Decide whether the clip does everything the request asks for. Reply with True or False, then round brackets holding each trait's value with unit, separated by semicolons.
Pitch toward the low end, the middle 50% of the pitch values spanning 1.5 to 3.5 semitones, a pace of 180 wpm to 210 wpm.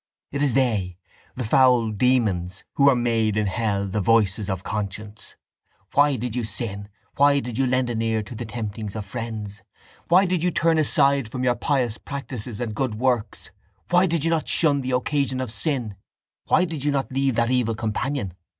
False (120 Hz; 4.2 semitones; 190 wpm)